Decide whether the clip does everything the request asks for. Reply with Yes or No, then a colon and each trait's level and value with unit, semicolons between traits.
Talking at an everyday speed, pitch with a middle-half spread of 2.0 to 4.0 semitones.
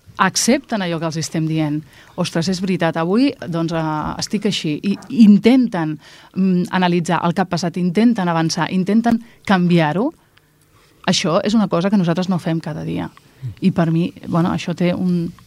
Yes: average, 160 wpm; average, 3.3 semitones